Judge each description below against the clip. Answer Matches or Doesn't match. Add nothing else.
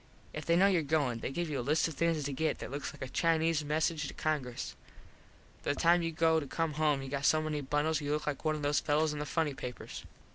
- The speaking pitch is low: Doesn't match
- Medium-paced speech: Doesn't match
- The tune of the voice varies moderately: Doesn't match